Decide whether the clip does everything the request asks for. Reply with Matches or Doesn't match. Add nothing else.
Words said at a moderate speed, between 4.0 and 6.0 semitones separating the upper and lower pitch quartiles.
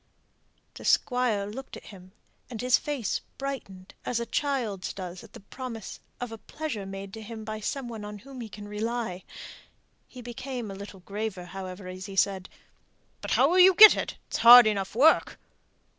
Matches